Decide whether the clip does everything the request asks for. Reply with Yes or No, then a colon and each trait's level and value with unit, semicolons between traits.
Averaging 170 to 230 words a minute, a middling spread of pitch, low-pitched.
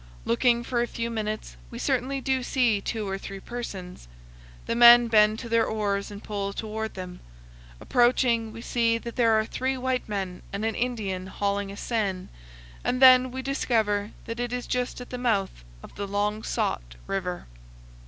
No: average, 180 wpm; average, 3.3 semitones; high, 225 Hz